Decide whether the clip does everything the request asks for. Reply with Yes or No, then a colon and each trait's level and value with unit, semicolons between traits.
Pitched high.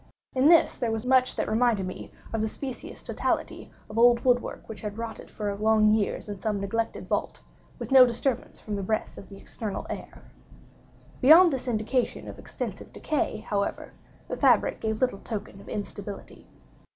Yes: high, 220 Hz